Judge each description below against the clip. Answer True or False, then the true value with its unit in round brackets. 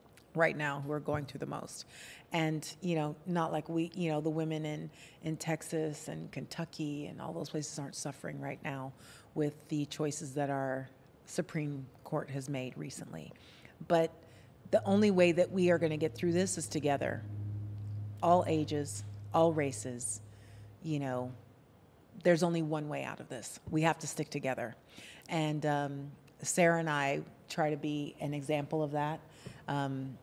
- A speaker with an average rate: True (170 wpm)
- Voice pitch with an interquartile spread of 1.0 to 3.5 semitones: True (2.8 semitones)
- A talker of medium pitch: True (150 Hz)